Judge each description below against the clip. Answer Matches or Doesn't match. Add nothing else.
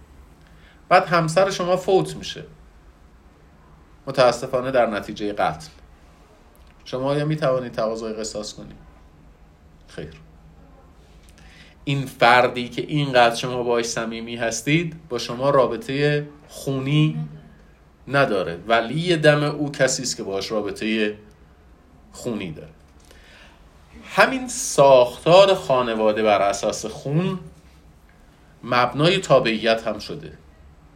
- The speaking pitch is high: Doesn't match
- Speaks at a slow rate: Matches